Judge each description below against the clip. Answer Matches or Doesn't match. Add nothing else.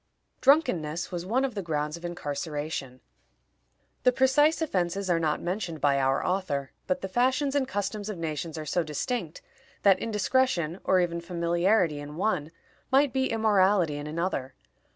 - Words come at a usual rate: Matches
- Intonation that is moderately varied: Doesn't match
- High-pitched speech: Doesn't match